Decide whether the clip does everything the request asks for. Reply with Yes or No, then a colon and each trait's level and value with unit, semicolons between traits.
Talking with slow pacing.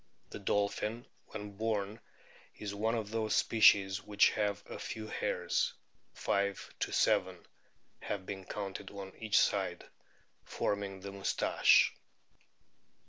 Yes: slow, 115 wpm